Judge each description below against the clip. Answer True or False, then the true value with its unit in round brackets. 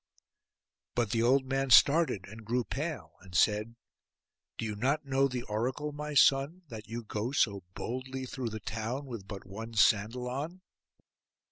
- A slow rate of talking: False (160 wpm)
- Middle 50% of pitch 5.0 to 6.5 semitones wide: False (3.9 semitones)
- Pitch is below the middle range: True (125 Hz)